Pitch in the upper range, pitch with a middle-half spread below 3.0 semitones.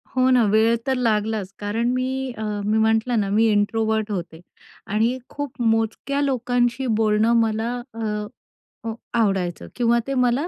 Yes: high, 225 Hz; narrow, 2.5 semitones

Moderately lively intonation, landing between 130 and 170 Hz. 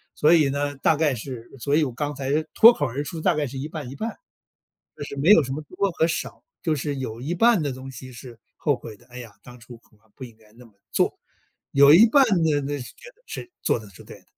Yes: average, 4.0 semitones; medium, 140 Hz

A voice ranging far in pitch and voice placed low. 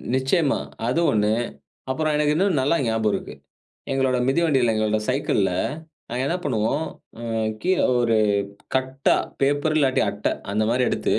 No: average, 4.5 semitones; low, 130 Hz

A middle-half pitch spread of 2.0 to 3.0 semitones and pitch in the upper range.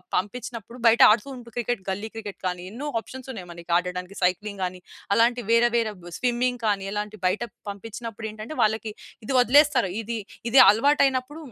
No: average, 3.5 semitones; high, 225 Hz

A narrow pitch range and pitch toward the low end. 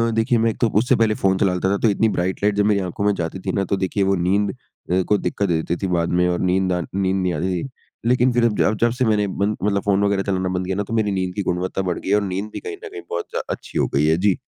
Yes: narrow, 2.2 semitones; low, 100 Hz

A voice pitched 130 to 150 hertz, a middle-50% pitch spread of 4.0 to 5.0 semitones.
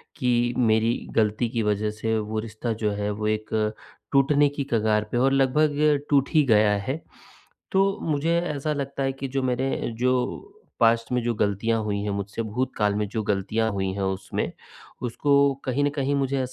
No: low, 120 Hz; average, 4.4 semitones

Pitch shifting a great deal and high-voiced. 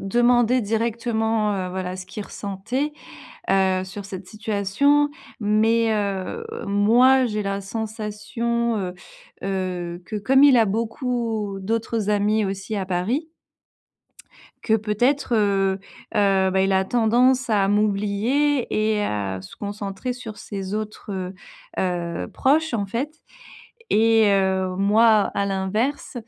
No: average, 3.1 semitones; high, 210 Hz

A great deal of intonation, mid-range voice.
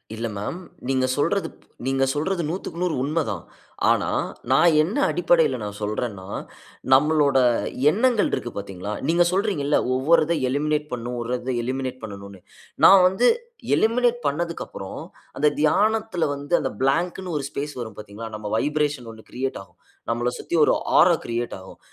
Yes: wide, 6.3 semitones; medium, 145 Hz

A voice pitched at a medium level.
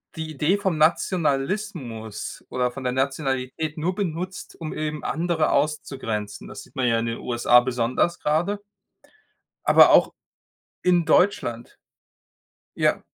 Yes: medium, 150 Hz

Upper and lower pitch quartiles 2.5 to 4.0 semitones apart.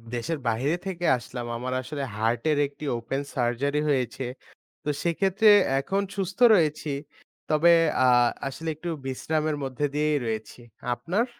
No: average, 4.6 semitones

